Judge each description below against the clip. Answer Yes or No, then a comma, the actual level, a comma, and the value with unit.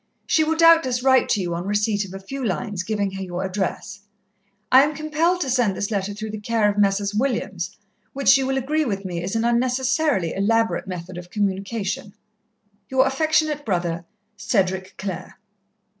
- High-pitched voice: Yes, high, 210 Hz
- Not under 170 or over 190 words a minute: Yes, average, 175 wpm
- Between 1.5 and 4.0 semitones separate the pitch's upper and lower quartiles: No, wide, 5.6 semitones